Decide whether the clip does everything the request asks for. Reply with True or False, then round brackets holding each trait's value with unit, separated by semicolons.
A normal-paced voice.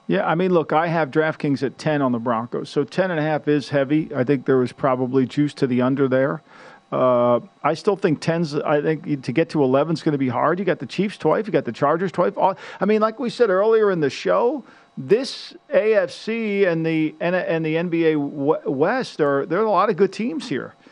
False (225 wpm)